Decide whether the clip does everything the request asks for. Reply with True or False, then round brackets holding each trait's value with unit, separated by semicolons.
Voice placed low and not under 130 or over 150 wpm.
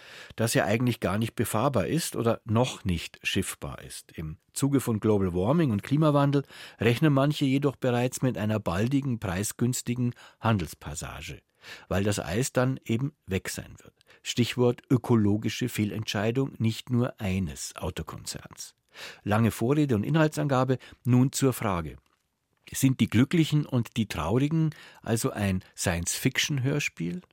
True (120 Hz; 135 wpm)